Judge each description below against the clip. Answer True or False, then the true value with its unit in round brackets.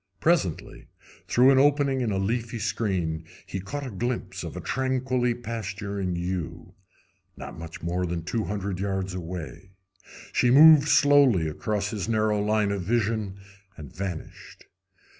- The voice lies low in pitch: True (105 Hz)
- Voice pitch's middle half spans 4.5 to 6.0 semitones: True (4.8 semitones)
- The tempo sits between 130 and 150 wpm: True (140 wpm)